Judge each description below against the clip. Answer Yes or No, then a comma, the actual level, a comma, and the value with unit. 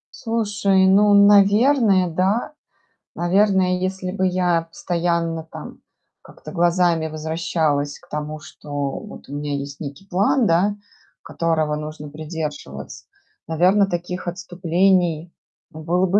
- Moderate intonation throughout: Yes, average, 3.4 semitones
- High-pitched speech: No, medium, 175 Hz